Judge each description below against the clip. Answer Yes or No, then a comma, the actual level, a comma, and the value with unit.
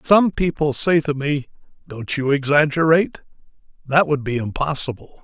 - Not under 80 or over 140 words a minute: Yes, slow, 135 wpm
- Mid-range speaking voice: Yes, medium, 145 Hz